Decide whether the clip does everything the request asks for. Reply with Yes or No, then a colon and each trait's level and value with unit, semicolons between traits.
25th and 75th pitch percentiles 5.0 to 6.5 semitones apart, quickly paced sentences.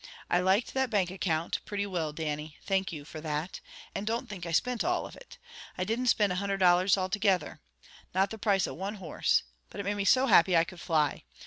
No: average, 3.4 semitones; fast, 225 wpm